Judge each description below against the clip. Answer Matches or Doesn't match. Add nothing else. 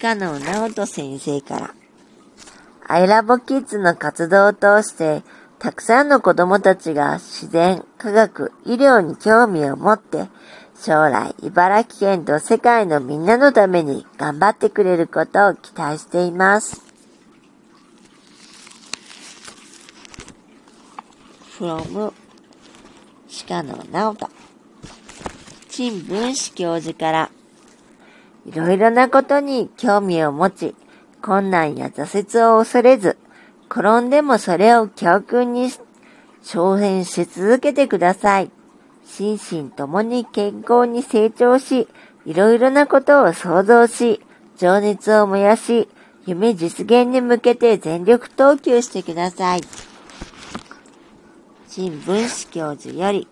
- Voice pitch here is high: Matches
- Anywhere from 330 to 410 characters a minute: Doesn't match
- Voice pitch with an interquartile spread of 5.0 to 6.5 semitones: Matches